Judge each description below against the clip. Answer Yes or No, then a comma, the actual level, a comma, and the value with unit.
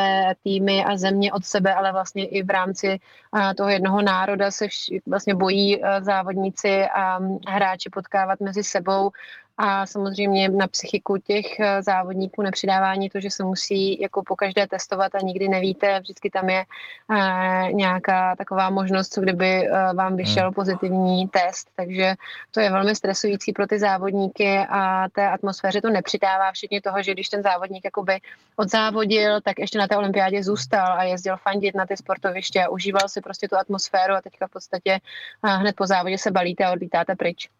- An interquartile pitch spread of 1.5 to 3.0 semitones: No, narrow, 0.9 semitones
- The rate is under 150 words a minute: No, average, 165 wpm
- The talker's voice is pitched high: Yes, high, 195 Hz